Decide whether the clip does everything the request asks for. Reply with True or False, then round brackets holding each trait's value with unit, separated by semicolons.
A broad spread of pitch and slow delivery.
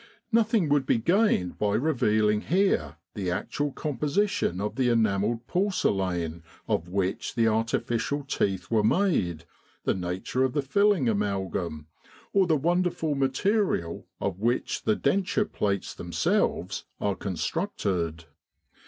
True (8.8 semitones; 125 wpm)